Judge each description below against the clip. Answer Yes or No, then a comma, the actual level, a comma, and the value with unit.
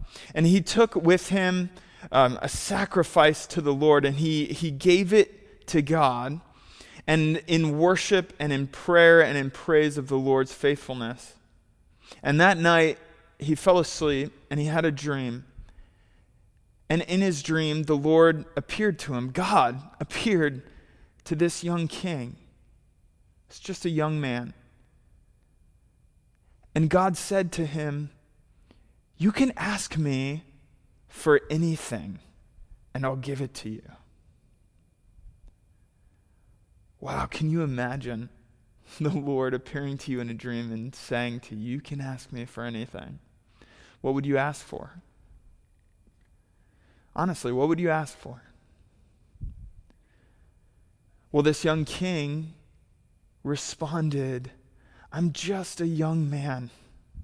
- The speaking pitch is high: No, medium, 145 Hz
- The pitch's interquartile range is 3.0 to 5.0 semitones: No, wide, 5.5 semitones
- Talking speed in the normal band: No, slow, 130 wpm